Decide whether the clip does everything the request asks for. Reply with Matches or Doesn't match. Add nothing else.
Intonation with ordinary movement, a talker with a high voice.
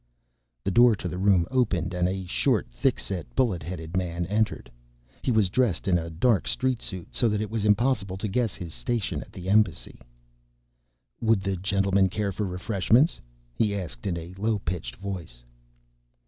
Doesn't match